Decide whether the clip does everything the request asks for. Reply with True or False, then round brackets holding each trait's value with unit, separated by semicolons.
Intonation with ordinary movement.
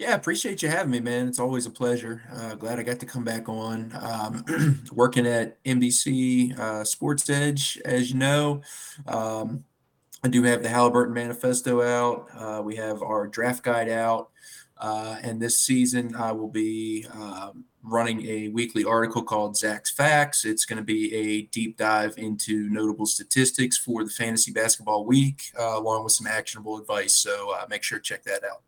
False (2.3 semitones)